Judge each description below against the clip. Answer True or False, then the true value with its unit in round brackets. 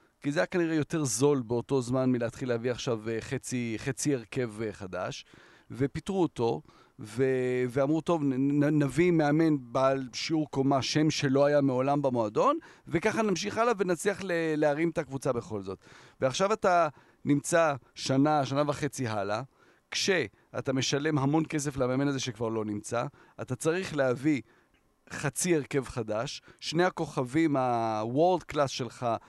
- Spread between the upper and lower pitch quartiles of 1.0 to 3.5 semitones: False (3.9 semitones)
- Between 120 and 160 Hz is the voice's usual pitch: True (140 Hz)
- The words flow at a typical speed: True (140 wpm)